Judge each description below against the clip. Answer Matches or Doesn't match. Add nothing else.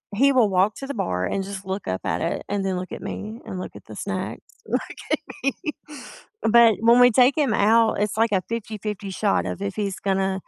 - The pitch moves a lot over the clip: Doesn't match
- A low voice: Doesn't match